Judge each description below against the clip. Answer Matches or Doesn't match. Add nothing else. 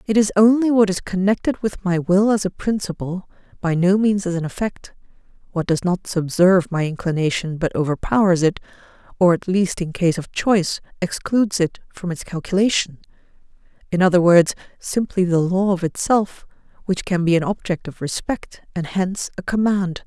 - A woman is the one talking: Matches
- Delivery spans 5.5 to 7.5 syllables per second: Doesn't match